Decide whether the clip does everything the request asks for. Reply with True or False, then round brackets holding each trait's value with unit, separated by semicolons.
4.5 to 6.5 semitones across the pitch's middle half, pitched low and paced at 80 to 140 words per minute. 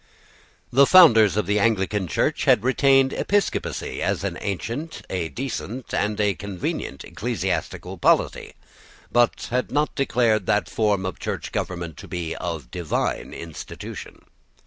True (5.5 semitones; 105 Hz; 135 wpm)